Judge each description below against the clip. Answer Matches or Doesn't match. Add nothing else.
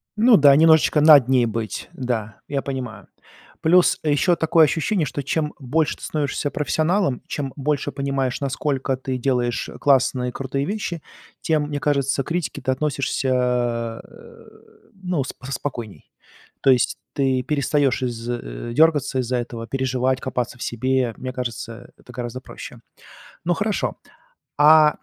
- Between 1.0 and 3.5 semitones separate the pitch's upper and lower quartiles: Matches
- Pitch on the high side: Doesn't match